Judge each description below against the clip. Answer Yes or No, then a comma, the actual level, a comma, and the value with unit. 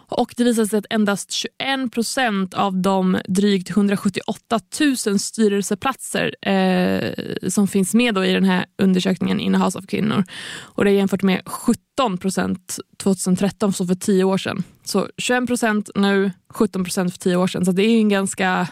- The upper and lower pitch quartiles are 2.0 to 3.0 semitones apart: Yes, narrow, 2.4 semitones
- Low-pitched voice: No, high, 195 Hz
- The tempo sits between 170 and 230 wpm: Yes, average, 175 wpm